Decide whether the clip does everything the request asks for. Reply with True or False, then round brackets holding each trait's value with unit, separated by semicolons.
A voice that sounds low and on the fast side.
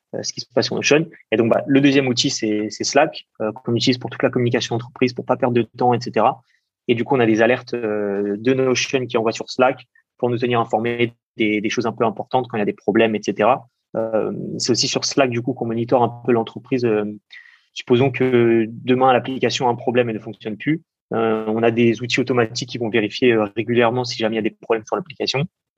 True (120 Hz; 240 wpm)